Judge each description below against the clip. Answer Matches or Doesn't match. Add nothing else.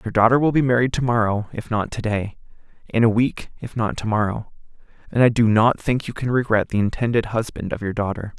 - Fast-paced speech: Matches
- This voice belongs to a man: Matches